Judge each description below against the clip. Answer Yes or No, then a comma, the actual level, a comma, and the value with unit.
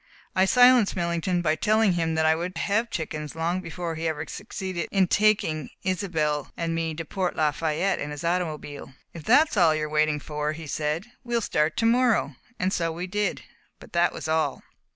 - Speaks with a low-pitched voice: No, medium, 165 Hz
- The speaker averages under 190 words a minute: No, average, 195 wpm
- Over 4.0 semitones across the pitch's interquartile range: No, average, 3.6 semitones